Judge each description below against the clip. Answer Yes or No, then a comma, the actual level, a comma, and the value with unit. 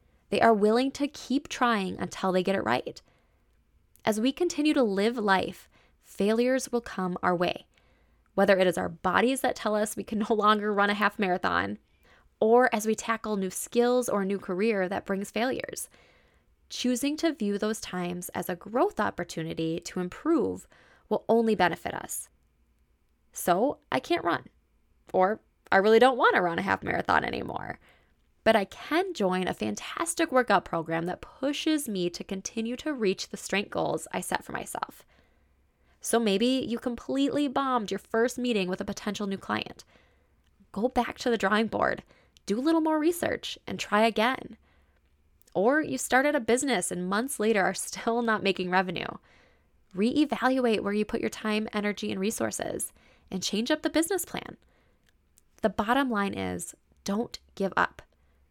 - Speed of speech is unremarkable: Yes, average, 170 wpm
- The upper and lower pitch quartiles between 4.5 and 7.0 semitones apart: Yes, average, 5.1 semitones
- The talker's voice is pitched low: No, high, 210 Hz